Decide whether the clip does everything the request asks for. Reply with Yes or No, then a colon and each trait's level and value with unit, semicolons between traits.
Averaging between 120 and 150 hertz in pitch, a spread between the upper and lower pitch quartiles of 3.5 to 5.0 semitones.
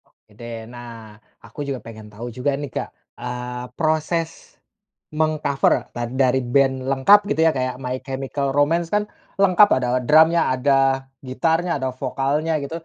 Yes: low, 135 Hz; average, 3.9 semitones